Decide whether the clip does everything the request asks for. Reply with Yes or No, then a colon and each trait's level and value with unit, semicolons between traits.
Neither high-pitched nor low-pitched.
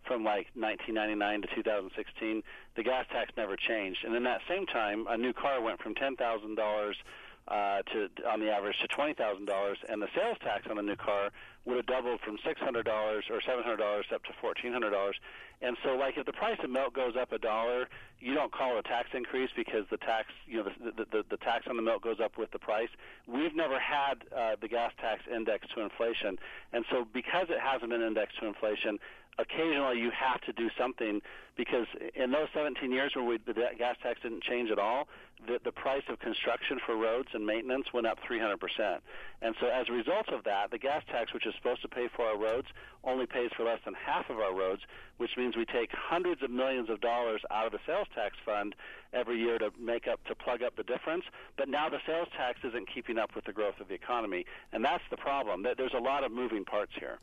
No: low, 120 Hz